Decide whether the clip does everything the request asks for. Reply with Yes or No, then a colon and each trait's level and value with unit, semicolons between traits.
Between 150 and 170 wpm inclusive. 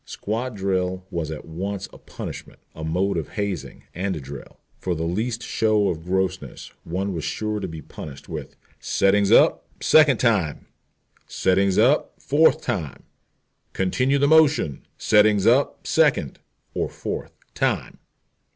No: average, 140 wpm